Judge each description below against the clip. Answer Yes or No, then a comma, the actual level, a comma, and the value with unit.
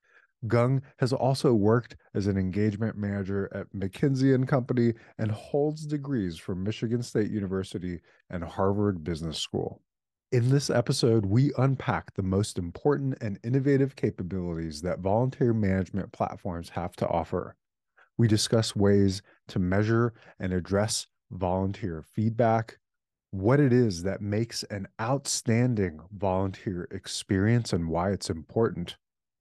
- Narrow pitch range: No, average, 4.1 semitones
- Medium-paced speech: No, slow, 130 wpm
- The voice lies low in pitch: Yes, low, 105 Hz